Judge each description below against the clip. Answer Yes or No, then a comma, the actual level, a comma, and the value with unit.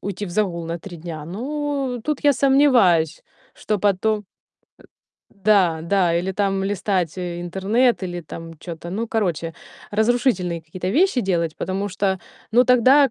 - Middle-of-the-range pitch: No, high, 195 Hz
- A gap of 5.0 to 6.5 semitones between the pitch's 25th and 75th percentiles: Yes, average, 5.3 semitones